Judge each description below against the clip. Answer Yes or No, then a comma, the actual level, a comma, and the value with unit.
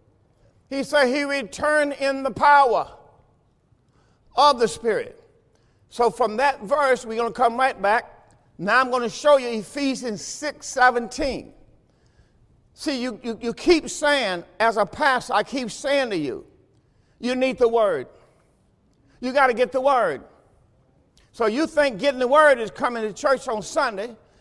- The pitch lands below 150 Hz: No, very high, 260 Hz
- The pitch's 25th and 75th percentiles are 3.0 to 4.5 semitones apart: Yes, average, 3.9 semitones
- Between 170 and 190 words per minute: No, average, 160 wpm